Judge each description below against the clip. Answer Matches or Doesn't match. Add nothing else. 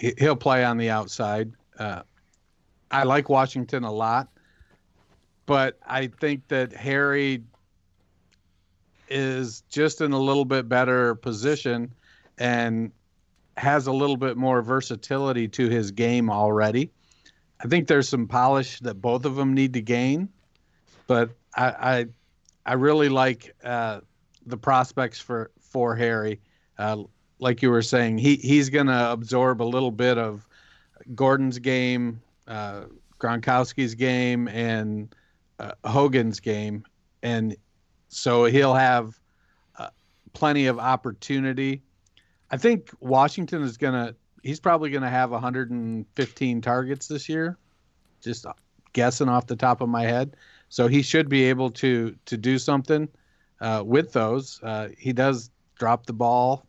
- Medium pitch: Doesn't match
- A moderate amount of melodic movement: Matches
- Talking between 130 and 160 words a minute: Matches